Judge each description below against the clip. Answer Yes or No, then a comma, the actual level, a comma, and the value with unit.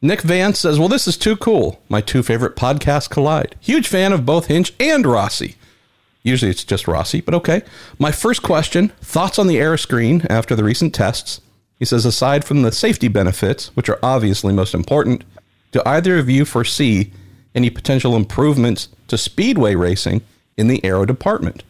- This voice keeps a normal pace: Yes, average, 180 wpm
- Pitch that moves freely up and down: Yes, wide, 6.1 semitones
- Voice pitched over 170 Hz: No, low, 125 Hz